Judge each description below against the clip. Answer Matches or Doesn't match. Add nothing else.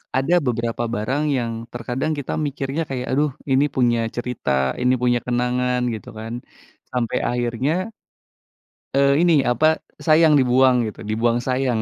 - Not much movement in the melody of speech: Matches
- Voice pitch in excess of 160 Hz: Doesn't match